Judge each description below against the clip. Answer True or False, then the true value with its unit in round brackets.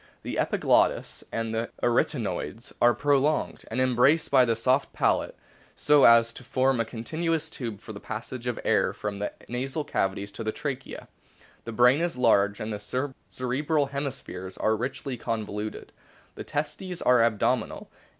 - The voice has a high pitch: False (125 Hz)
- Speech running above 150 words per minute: True (160 wpm)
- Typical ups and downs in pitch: True (3.8 semitones)